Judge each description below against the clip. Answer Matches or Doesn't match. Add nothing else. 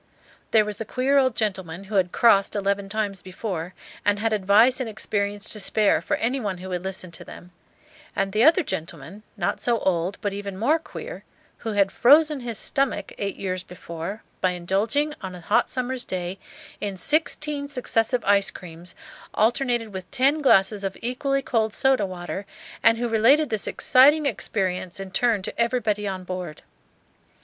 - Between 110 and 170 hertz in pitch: Doesn't match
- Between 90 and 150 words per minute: Doesn't match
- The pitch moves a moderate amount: Matches